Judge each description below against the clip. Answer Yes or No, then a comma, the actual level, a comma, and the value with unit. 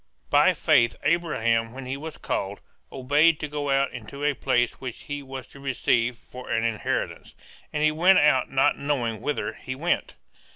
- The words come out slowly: No, average, 175 wpm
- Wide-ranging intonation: No, average, 3.4 semitones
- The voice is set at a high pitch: No, low, 135 Hz